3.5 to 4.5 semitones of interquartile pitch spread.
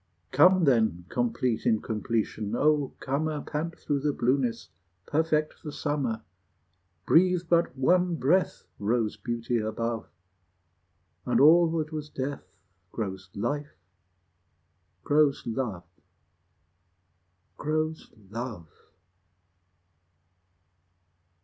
No: average, 5.1 semitones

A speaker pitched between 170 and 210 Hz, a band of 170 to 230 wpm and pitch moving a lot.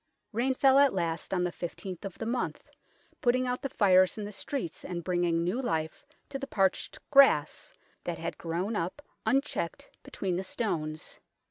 Yes: high, 190 Hz; average, 175 wpm; wide, 6.5 semitones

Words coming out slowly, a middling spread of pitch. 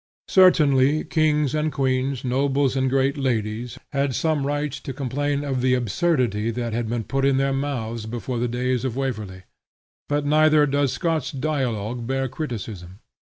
No: average, 160 wpm; average, 3.1 semitones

